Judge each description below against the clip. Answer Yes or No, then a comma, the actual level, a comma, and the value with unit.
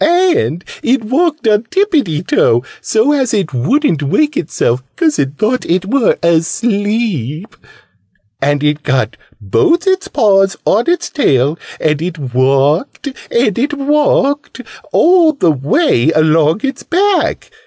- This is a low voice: No, high, 210 Hz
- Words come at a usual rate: No, slow, 130 wpm